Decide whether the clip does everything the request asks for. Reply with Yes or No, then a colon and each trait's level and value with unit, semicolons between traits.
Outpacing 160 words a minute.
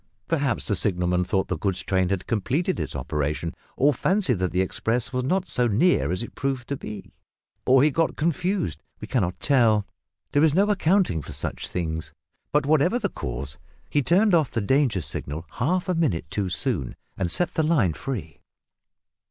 Yes: average, 185 wpm